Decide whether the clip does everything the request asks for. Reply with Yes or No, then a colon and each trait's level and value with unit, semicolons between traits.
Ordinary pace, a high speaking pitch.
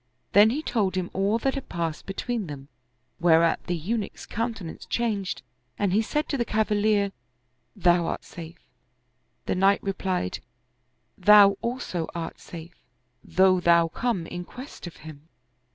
Yes: average, 155 wpm; high, 195 Hz